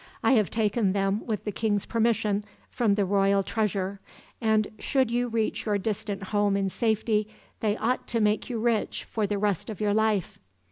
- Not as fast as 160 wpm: No, average, 185 wpm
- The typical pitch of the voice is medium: No, high, 210 Hz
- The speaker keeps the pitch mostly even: Yes, narrow, 1.8 semitones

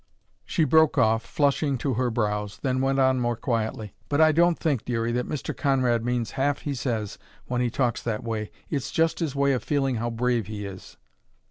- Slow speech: No, fast, 205 wpm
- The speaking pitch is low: Yes, low, 125 Hz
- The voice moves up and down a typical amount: Yes, average, 3.6 semitones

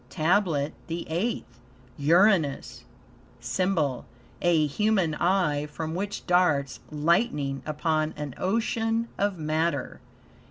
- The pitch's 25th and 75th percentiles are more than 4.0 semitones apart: Yes, average, 4.5 semitones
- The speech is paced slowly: Yes, slow, 95 wpm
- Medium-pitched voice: Yes, medium, 165 Hz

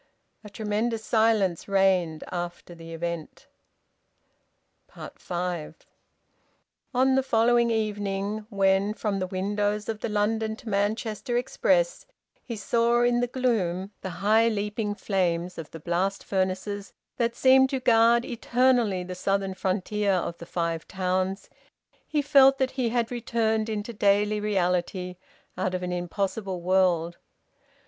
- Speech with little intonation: No, average, 3.8 semitones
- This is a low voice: No, high, 205 Hz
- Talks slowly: Yes, slow, 130 wpm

